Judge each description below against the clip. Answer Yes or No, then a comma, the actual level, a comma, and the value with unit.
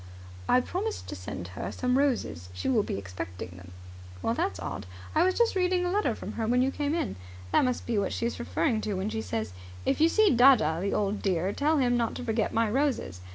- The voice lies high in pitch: Yes, high, 230 Hz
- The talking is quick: Yes, fast, 225 wpm